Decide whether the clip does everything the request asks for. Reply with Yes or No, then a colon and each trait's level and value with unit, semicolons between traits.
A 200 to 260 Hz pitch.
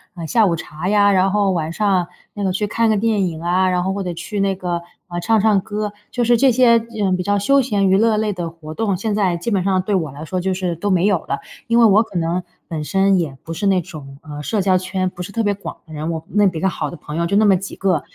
No: high, 190 Hz